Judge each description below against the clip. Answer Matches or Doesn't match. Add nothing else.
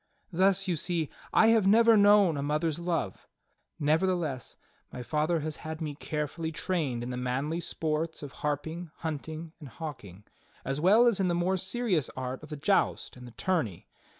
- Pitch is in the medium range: Matches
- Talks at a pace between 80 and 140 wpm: Doesn't match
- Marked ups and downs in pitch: Doesn't match